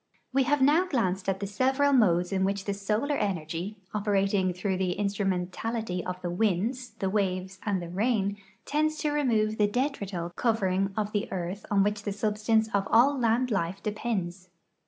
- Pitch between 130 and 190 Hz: No, high, 205 Hz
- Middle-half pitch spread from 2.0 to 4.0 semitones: Yes, average, 3.4 semitones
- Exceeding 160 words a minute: Yes, average, 175 wpm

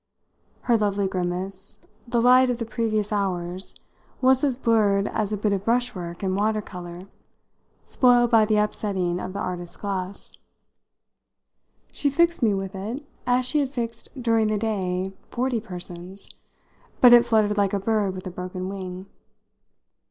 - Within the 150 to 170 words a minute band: Yes, average, 155 wpm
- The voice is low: No, high, 210 Hz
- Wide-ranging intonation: No, average, 3.8 semitones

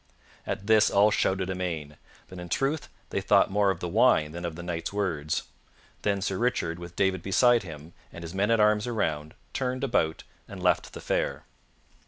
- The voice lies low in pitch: Yes, very low, 95 Hz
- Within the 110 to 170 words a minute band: No, average, 190 wpm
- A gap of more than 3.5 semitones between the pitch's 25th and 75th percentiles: Yes, average, 4.1 semitones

